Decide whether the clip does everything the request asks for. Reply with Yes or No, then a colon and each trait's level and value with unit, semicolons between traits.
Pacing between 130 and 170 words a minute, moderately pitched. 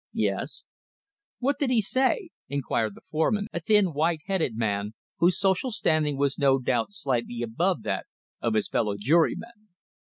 Yes: average, 155 wpm; medium, 155 Hz